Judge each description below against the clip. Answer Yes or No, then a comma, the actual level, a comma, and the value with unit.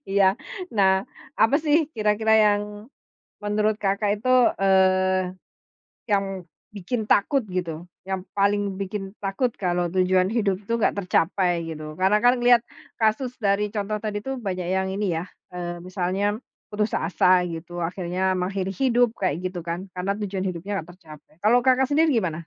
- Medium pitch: No, high, 195 Hz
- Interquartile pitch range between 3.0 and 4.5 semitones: No, narrow, 2.6 semitones